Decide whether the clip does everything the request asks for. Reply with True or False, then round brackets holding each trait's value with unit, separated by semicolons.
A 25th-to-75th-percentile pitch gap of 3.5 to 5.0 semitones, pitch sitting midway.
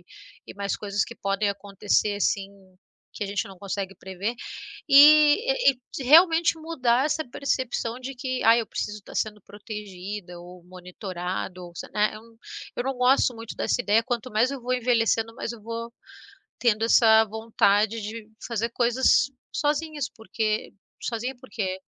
False (3.8 semitones; 225 Hz)